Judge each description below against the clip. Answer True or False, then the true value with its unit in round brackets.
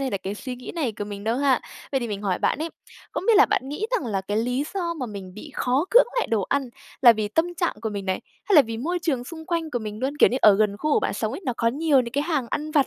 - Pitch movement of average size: False (6.2 semitones)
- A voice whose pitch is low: False (255 Hz)